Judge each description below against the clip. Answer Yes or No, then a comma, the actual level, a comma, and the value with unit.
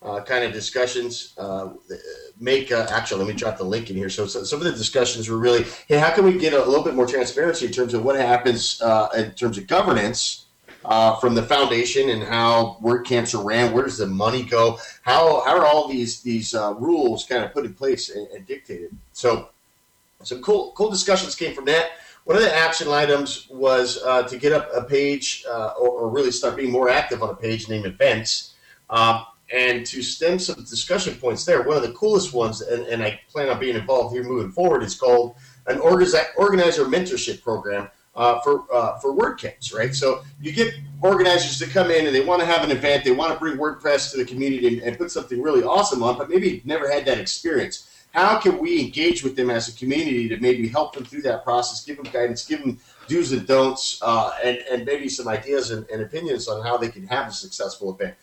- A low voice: Yes, low, 130 Hz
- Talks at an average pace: No, fast, 225 wpm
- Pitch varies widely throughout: Yes, wide, 5.9 semitones